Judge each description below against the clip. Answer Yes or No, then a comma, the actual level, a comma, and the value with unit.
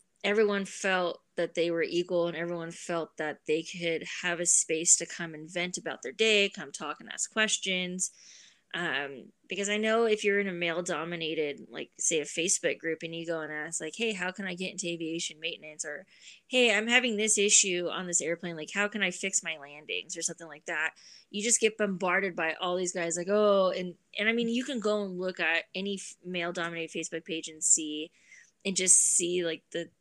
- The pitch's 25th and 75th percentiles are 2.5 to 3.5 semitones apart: Yes, average, 3.2 semitones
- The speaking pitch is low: No, medium, 175 Hz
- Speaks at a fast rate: Yes, fast, 210 wpm